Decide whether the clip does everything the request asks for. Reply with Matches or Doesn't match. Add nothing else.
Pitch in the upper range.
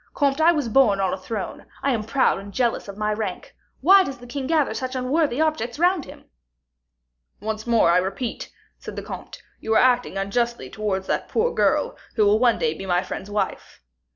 Matches